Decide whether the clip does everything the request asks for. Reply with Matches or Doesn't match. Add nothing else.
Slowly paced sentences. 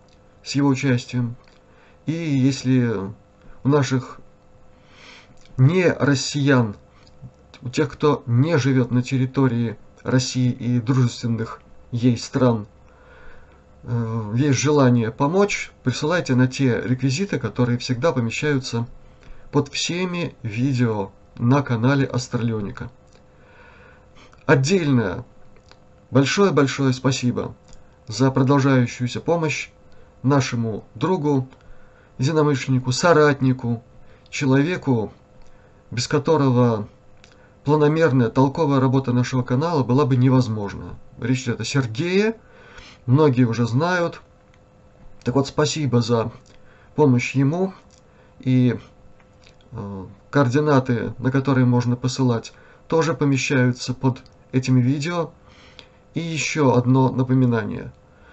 Matches